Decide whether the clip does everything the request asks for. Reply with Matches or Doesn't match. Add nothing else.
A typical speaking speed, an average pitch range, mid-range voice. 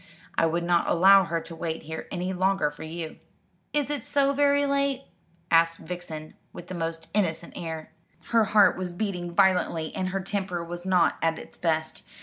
Matches